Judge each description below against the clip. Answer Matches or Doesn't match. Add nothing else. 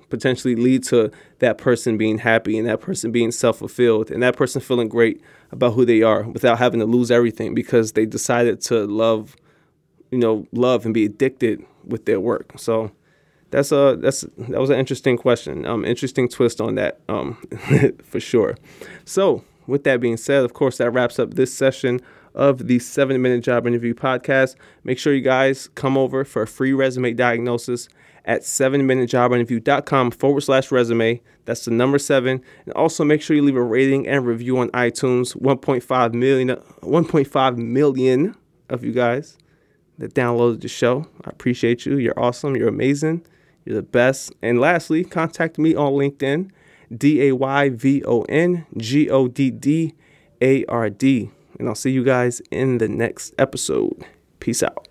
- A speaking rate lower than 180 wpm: Matches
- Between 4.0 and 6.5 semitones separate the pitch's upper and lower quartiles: Doesn't match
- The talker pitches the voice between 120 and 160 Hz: Matches